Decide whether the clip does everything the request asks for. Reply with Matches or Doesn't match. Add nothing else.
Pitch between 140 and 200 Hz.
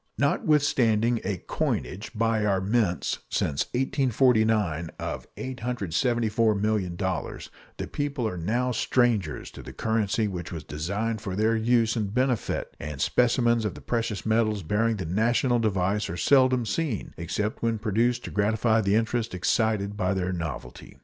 Doesn't match